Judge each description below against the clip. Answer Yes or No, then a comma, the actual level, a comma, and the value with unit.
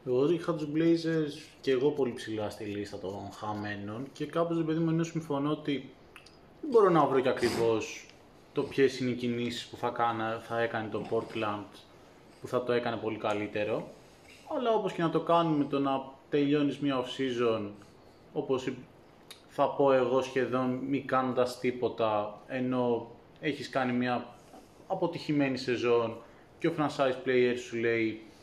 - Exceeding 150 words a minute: Yes, average, 160 wpm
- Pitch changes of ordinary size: Yes, average, 3.8 semitones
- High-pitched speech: No, low, 125 Hz